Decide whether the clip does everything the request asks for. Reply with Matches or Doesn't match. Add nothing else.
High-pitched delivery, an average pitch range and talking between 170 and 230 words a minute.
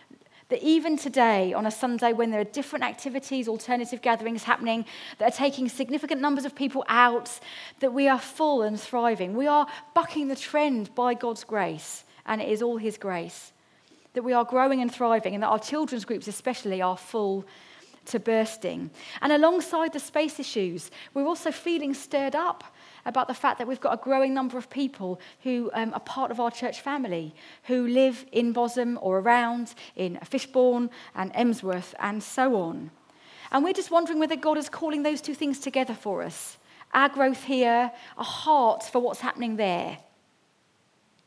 Matches